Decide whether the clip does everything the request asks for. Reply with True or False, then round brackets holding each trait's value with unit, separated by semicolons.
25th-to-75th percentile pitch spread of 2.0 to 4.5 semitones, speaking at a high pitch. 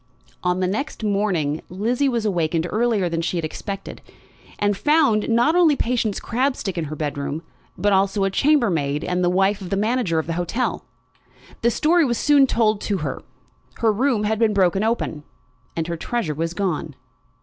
False (5.4 semitones; 200 Hz)